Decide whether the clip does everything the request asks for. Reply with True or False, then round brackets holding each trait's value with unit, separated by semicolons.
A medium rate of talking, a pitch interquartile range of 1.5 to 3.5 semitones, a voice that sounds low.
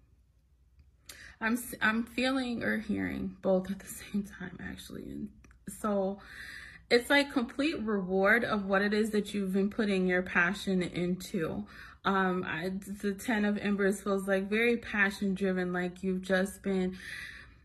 False (145 wpm; 2.6 semitones; 195 Hz)